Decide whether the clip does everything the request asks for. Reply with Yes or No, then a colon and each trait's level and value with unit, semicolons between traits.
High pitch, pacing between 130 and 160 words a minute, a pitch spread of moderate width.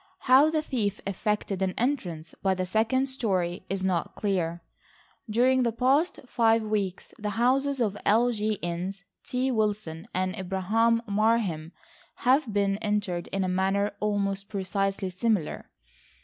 Yes: high, 205 Hz; average, 140 wpm; average, 3.7 semitones